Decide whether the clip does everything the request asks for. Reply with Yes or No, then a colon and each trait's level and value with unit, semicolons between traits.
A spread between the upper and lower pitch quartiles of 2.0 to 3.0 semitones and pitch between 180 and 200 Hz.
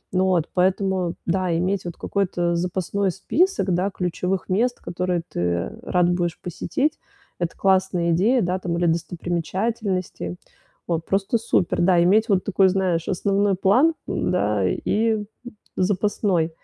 Yes: narrow, 2.4 semitones; medium, 185 Hz